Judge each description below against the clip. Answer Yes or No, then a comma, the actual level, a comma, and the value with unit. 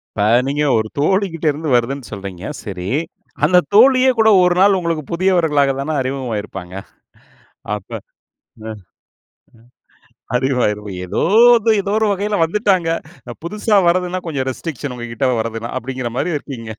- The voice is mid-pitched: Yes, medium, 150 Hz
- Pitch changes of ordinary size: No, wide, 7.3 semitones